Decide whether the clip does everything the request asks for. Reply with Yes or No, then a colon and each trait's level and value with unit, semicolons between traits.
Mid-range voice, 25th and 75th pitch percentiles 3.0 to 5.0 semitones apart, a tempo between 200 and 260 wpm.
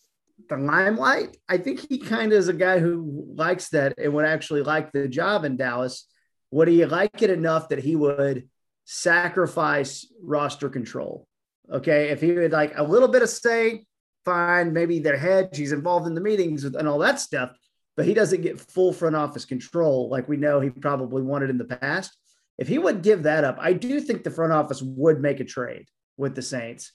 Yes: medium, 155 Hz; average, 4.4 semitones; fast, 205 wpm